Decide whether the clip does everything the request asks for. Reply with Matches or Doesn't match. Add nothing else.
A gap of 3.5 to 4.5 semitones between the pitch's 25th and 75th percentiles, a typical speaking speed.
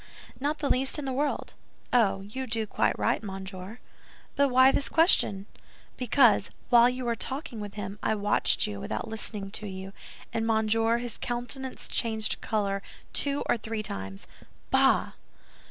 Matches